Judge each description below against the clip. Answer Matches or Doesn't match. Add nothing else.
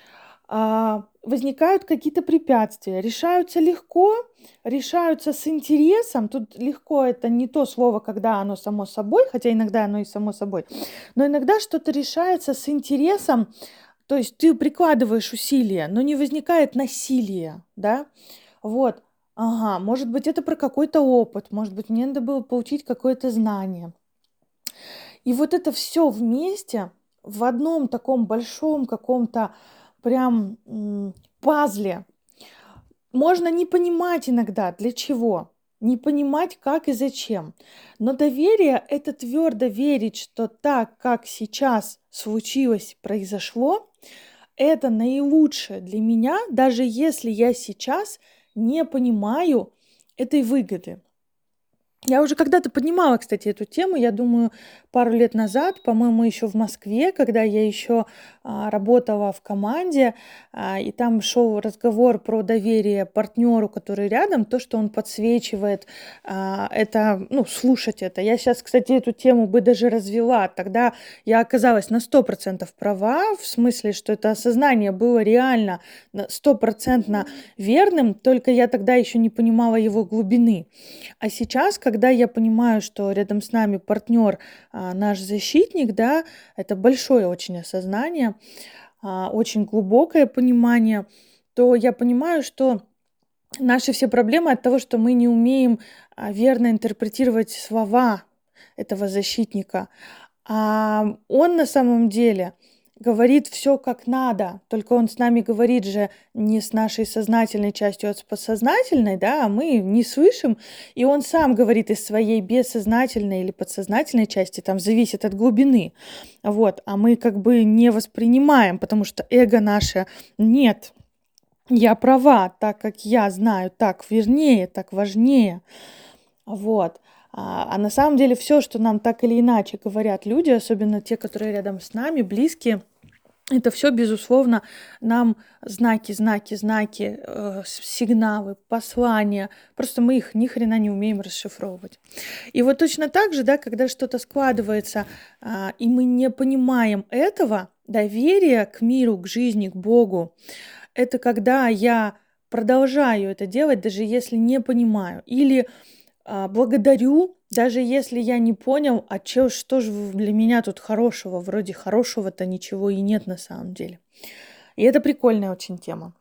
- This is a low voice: Doesn't match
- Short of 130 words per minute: Doesn't match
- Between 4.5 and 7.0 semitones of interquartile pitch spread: Doesn't match